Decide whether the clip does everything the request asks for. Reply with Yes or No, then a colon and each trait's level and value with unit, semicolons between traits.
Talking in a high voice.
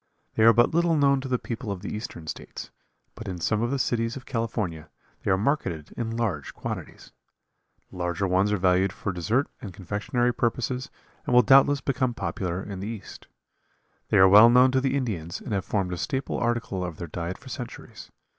No: low, 110 Hz